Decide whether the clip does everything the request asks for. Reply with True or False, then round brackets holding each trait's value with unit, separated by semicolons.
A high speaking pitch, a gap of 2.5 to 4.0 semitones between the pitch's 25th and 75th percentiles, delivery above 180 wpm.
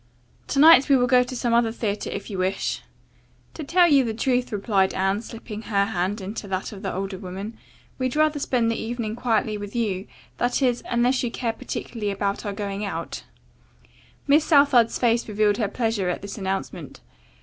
True (225 Hz; 3.7 semitones; 190 wpm)